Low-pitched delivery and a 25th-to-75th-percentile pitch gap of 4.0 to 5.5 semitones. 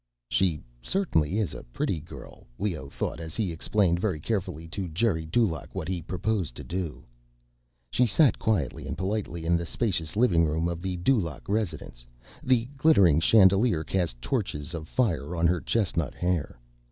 Yes: very low, 90 Hz; average, 4.6 semitones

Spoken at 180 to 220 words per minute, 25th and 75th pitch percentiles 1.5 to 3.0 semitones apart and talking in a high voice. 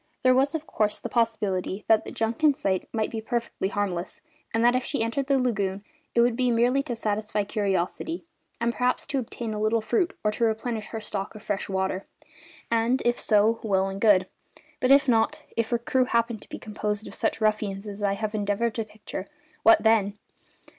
Yes: fast, 205 wpm; average, 2.7 semitones; high, 220 Hz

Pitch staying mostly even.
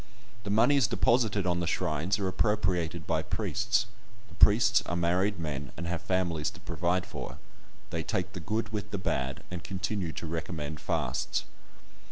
No: average, 3.9 semitones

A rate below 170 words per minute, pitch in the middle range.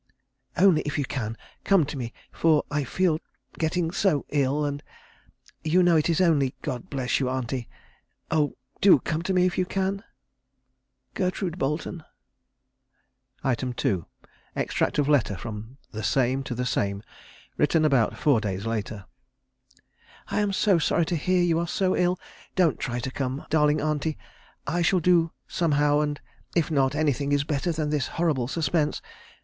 Yes: average, 160 wpm; medium, 150 Hz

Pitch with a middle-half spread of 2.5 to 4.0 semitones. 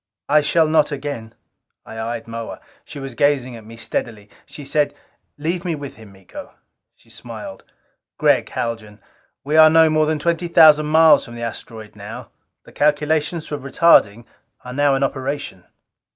No: average, 4.9 semitones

